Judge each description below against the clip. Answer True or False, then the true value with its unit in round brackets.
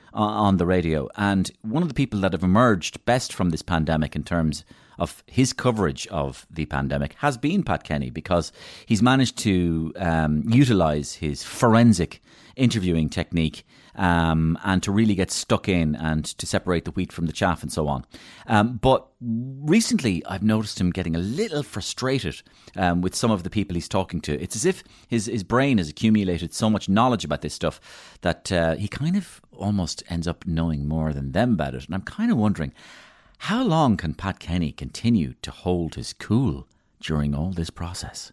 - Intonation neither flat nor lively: False (5.7 semitones)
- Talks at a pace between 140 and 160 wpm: False (190 wpm)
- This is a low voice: True (90 Hz)